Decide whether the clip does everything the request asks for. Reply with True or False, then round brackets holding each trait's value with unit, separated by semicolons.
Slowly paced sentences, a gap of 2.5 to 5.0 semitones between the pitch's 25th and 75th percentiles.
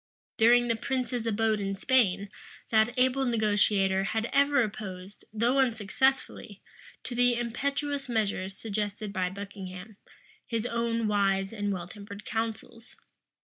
True (125 wpm; 3.3 semitones)